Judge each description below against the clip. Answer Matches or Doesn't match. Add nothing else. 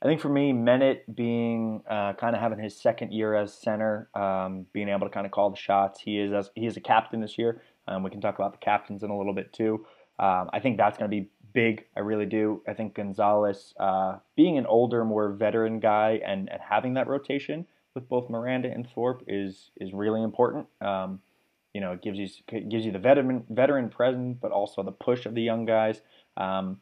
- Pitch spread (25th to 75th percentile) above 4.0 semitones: Doesn't match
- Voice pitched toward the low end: Matches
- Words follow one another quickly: Matches